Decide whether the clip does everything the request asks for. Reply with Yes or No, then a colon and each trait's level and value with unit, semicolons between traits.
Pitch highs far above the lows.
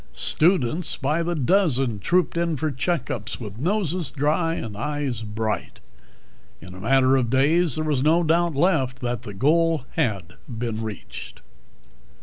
Yes: wide, 6.1 semitones